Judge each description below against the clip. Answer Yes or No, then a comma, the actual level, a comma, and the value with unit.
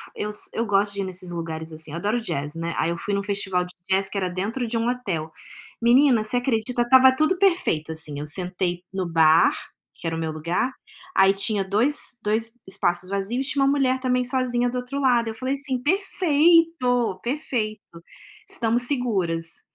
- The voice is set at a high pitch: Yes, high, 220 Hz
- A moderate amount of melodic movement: No, wide, 6.0 semitones